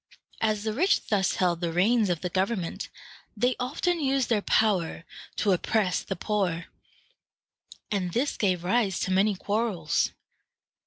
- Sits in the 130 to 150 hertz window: No, high, 205 Hz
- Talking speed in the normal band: Yes, average, 145 wpm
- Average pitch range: Yes, average, 4.1 semitones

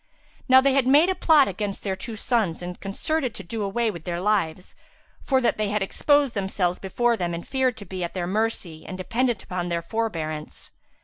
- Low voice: No, high, 205 Hz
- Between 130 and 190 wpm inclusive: No, average, 200 wpm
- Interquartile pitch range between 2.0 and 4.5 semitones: No, average, 5.1 semitones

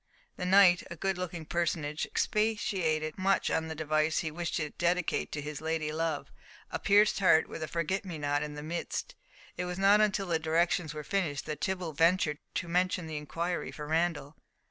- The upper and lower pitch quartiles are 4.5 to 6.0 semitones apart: No, average, 2.9 semitones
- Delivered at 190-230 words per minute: Yes, average, 195 wpm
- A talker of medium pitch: Yes, medium, 165 Hz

